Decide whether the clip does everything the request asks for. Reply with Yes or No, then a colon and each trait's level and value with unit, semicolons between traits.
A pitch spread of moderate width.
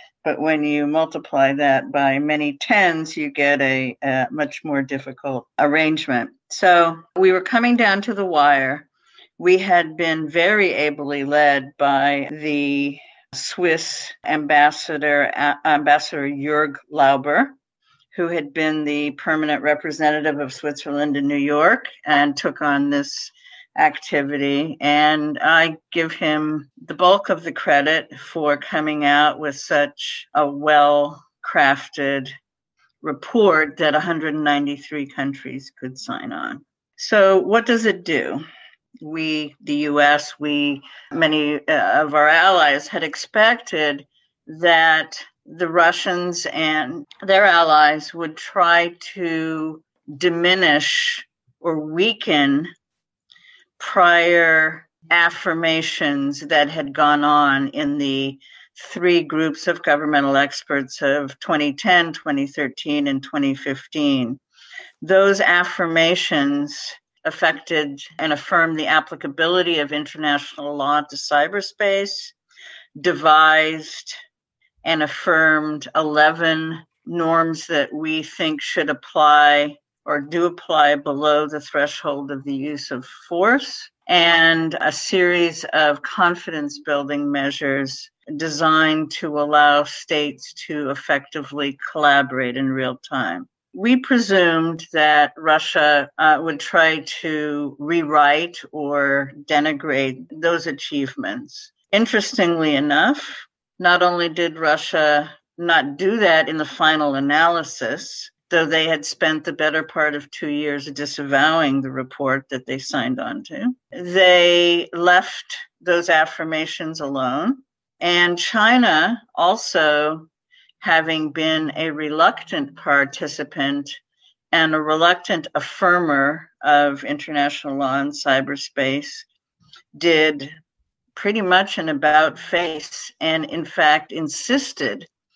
Yes: average, 3.0 semitones